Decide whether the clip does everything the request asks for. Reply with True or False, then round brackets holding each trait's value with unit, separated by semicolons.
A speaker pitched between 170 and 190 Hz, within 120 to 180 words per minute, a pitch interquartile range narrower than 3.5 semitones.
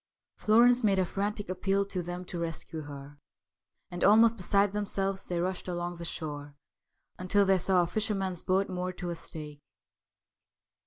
True (185 Hz; 160 wpm; 2.5 semitones)